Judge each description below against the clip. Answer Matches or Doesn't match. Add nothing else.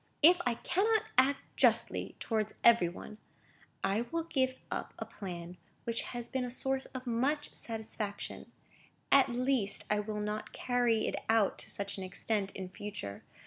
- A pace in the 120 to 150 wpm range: Doesn't match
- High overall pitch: Matches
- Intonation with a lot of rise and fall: Doesn't match